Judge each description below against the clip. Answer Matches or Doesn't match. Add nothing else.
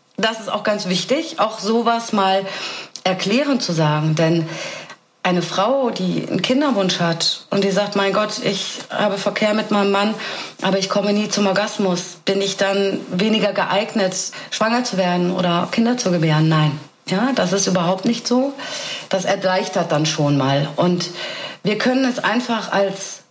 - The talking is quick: Doesn't match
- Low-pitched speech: Doesn't match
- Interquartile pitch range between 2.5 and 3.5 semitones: Matches